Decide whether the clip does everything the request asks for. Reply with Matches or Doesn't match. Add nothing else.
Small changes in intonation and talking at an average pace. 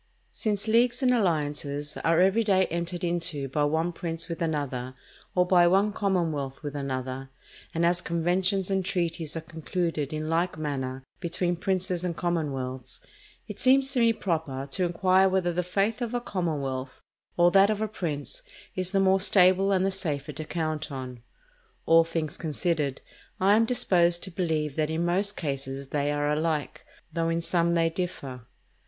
Doesn't match